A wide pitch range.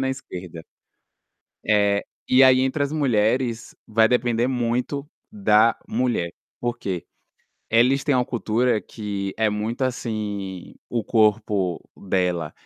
No: average, 3.7 semitones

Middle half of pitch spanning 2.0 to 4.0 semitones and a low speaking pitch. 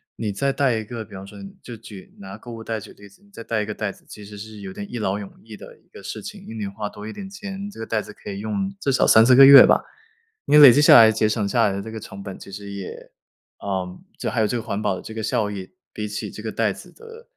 Yes: average, 3.1 semitones; low, 110 Hz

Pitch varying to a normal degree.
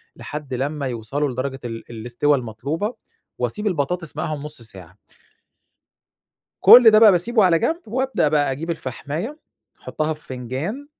No: wide, 5.9 semitones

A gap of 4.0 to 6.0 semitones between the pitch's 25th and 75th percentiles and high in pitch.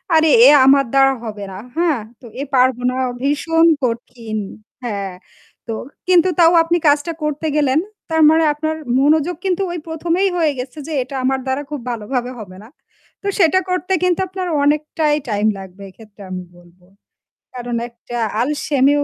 Yes: average, 5.2 semitones; very high, 280 Hz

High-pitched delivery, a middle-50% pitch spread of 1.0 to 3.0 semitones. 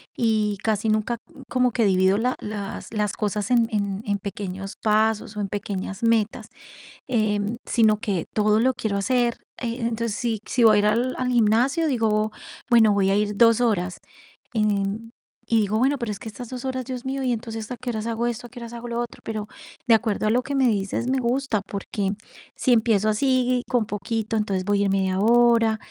Yes: high, 220 Hz; narrow, 2.6 semitones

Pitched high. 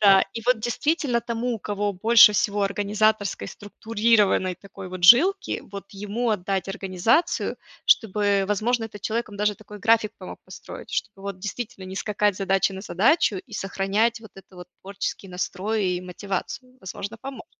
Yes: high, 205 Hz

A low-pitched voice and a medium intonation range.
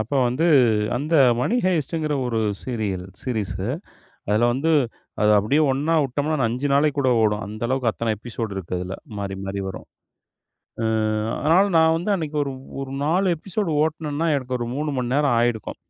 No: low, 130 Hz; wide, 6.1 semitones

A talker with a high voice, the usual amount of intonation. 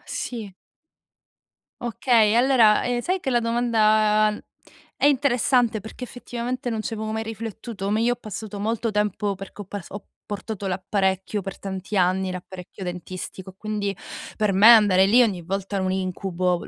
Yes: high, 210 Hz; average, 3.2 semitones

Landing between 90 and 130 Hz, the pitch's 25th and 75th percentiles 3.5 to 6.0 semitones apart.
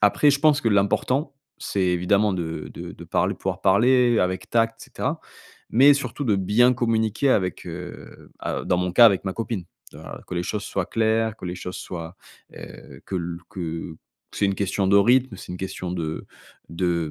Yes: low, 100 Hz; average, 4.2 semitones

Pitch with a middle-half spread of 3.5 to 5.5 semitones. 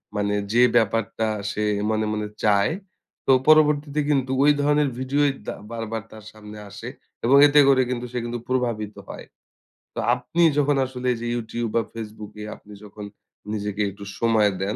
Yes: average, 3.8 semitones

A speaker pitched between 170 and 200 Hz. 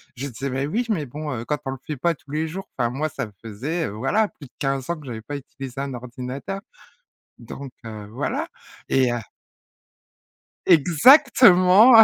No: medium, 140 Hz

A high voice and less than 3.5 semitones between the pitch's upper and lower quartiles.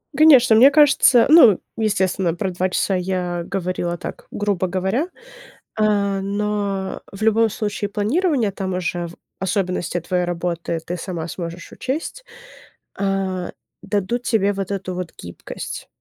Yes: high, 195 Hz; average, 3.1 semitones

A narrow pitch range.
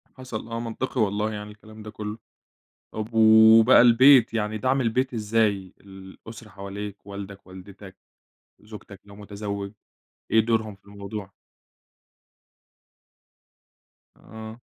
Yes: narrow, 1.9 semitones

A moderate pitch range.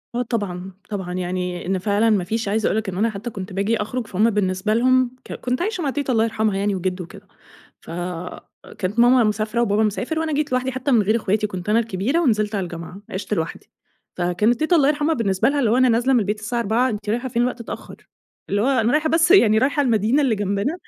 Yes: average, 4.3 semitones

